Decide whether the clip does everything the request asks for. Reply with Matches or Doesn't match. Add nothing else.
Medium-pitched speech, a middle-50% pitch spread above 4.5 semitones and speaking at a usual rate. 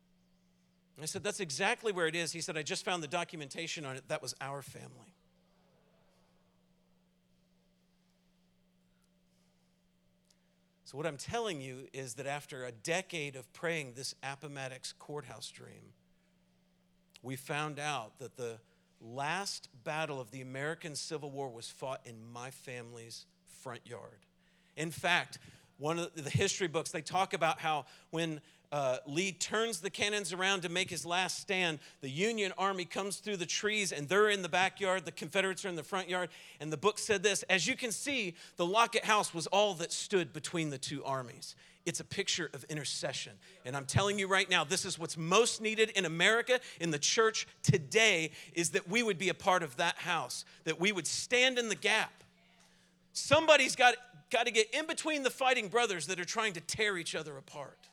Matches